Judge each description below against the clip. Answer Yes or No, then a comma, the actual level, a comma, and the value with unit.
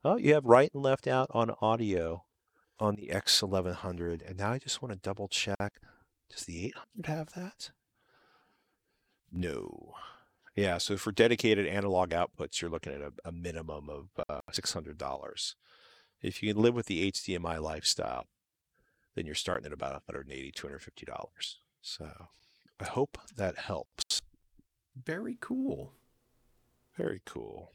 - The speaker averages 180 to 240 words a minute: No, average, 140 wpm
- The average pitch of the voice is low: Yes, low, 100 Hz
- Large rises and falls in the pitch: Yes, wide, 5.9 semitones